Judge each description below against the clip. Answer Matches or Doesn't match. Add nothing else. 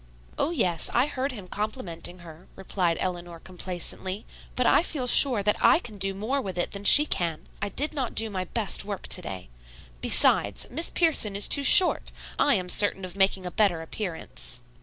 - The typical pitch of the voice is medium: Doesn't match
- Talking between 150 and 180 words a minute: Doesn't match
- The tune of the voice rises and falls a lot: Matches